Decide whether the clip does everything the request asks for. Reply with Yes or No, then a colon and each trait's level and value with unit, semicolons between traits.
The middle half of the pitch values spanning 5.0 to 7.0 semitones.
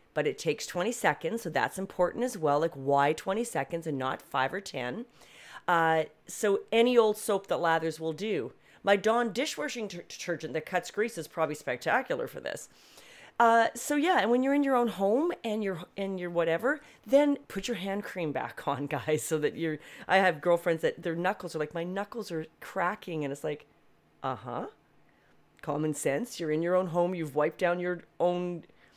Yes: wide, 5.6 semitones